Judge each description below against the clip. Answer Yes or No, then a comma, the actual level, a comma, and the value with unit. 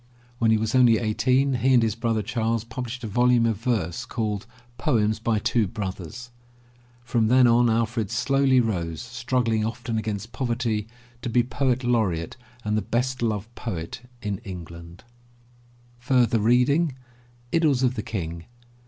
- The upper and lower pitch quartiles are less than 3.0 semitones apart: Yes, narrow, 2.5 semitones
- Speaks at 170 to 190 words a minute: No, average, 145 wpm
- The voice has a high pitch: No, low, 115 Hz